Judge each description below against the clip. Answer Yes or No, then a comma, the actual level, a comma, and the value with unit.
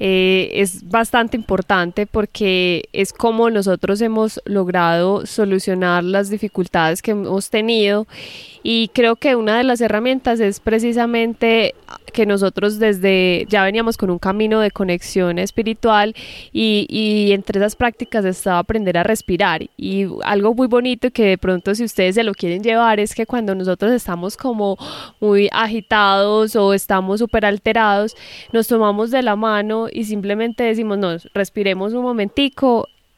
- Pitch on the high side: Yes, high, 210 Hz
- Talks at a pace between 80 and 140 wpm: No, average, 150 wpm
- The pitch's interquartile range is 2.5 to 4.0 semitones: Yes, average, 2.8 semitones